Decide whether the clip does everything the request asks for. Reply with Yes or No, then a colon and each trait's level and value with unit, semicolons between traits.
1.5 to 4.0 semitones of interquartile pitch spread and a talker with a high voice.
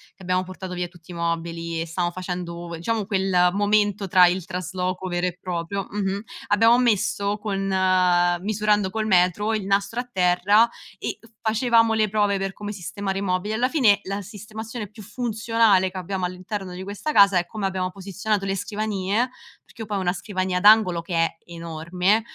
Yes: average, 2.7 semitones; high, 195 Hz